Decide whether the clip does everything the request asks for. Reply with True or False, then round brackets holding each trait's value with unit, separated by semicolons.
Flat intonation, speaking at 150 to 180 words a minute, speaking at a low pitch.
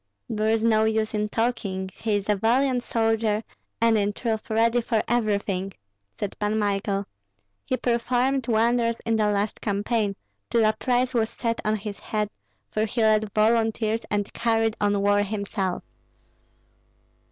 False (1.9 semitones; 155 wpm; 220 Hz)